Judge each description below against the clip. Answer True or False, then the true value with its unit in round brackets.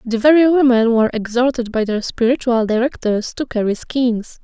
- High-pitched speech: True (240 Hz)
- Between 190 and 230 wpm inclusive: False (160 wpm)